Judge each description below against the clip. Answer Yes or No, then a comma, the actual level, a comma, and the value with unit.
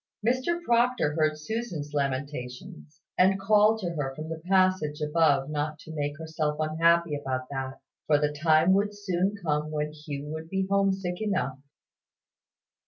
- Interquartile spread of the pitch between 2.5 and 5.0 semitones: Yes, average, 4.4 semitones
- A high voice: No, medium, 155 Hz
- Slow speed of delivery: No, average, 150 wpm